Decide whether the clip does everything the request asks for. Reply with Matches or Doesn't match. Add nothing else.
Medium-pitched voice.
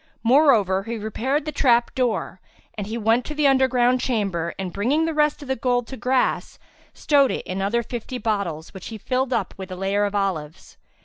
Doesn't match